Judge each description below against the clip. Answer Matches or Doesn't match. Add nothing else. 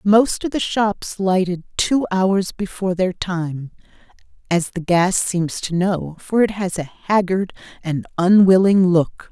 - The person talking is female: Matches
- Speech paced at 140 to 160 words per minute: Matches